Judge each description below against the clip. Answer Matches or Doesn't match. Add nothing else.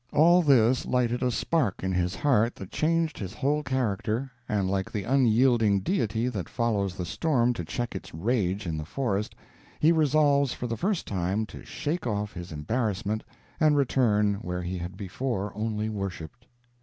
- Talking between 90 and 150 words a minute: Doesn't match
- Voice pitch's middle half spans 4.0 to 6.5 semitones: Matches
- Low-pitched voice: Matches